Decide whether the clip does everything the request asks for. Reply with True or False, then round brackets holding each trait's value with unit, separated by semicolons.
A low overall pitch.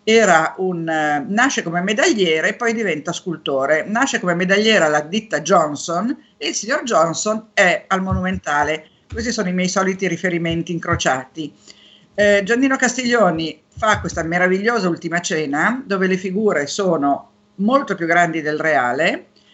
False (180 Hz)